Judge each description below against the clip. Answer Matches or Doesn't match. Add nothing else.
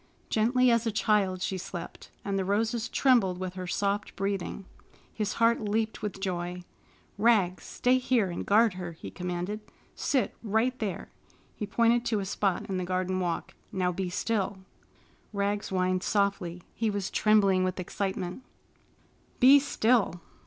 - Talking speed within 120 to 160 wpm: Matches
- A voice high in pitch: Matches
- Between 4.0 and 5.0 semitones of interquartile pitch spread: Doesn't match